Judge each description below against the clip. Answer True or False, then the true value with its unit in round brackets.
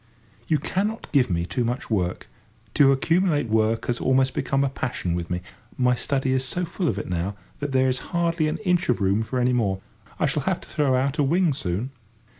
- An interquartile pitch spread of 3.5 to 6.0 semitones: True (5.2 semitones)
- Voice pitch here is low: True (130 Hz)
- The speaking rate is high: True (220 wpm)